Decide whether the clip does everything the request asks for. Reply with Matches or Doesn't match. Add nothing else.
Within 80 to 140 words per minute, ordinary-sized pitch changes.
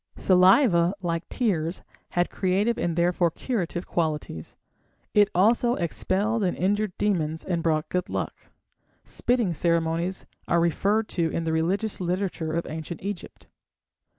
Matches